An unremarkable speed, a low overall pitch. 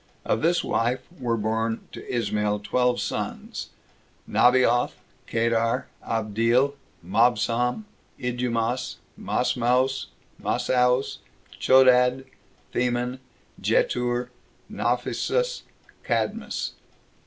No: slow, 75 wpm; low, 125 Hz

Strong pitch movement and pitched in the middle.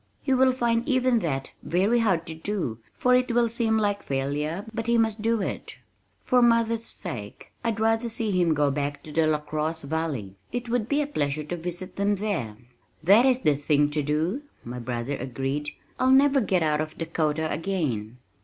Yes: wide, 7.7 semitones; medium, 175 Hz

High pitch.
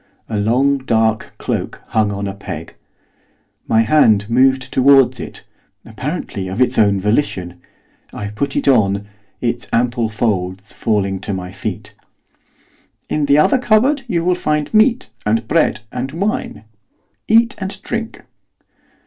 No: low, 120 Hz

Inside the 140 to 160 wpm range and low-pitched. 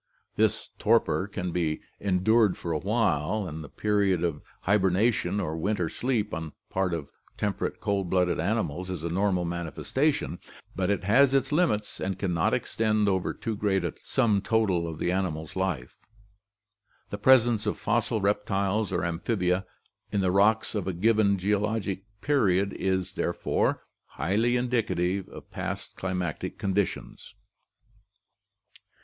Yes: average, 150 wpm; very low, 95 Hz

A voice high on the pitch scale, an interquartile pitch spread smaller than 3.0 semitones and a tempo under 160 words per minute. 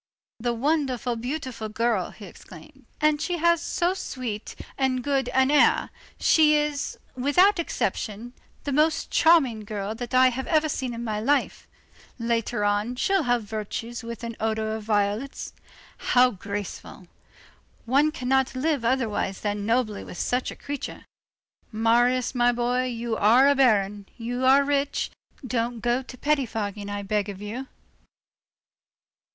No: high, 245 Hz; average, 3.8 semitones; average, 145 wpm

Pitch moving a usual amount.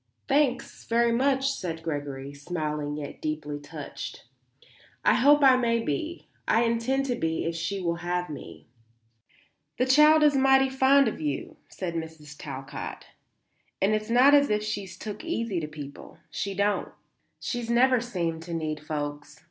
No: wide, 8.7 semitones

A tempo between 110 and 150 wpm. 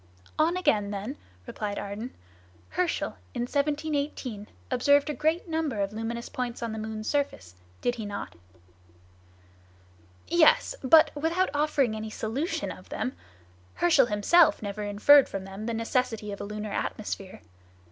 Yes: average, 140 wpm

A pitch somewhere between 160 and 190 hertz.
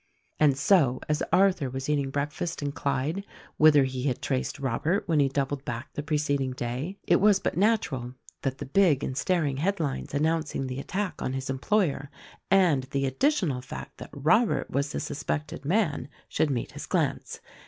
No: medium, 145 Hz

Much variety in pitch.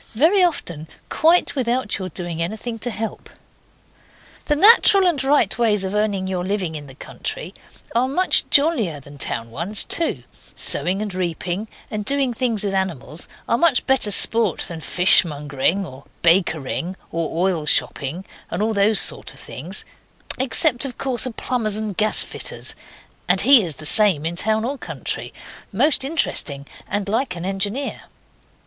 Yes: wide, 6.4 semitones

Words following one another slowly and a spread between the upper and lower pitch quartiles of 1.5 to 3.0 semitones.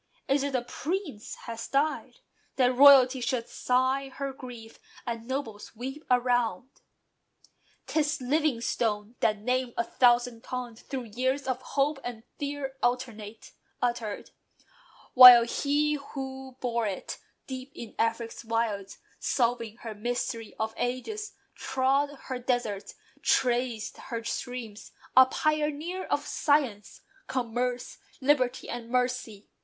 Yes: slow, 120 wpm; average, 2.7 semitones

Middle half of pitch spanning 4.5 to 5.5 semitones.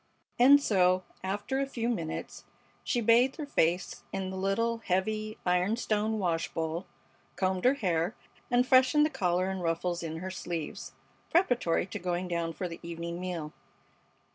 Yes: average, 5.1 semitones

